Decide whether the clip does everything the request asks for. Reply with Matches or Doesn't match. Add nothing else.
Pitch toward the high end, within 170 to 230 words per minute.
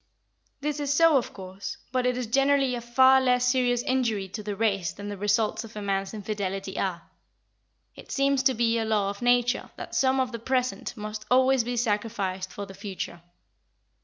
Matches